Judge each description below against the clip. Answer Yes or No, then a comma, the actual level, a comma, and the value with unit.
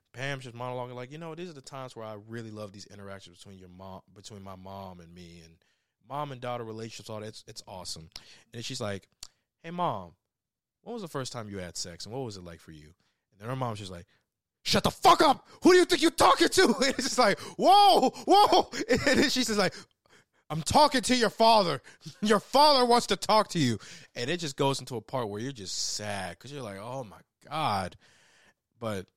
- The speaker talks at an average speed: No, fast, 230 wpm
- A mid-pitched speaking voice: No, low, 125 Hz